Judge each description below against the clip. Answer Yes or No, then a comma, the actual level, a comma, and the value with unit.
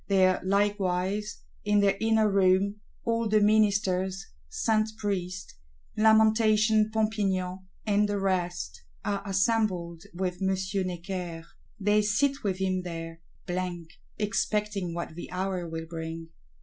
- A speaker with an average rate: No, slow, 120 wpm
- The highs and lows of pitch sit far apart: No, average, 2.8 semitones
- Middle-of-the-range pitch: No, high, 195 Hz